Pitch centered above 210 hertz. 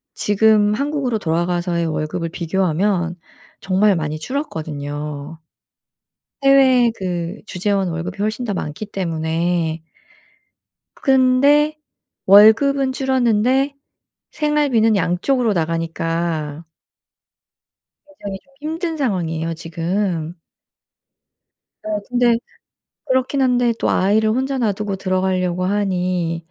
No: high, 195 Hz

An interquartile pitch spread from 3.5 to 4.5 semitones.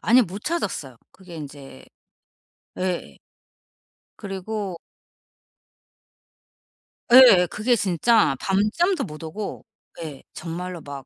No: average, 5.3 semitones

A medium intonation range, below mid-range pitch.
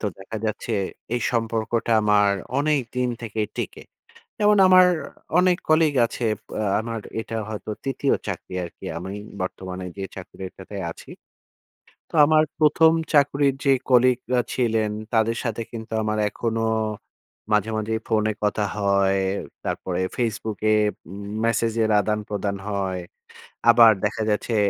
Yes: average, 3.3 semitones; low, 110 Hz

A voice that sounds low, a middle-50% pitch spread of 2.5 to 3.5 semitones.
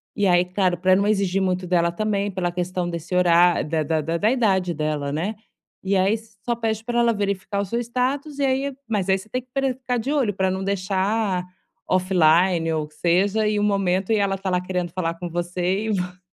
No: high, 190 Hz; average, 3.2 semitones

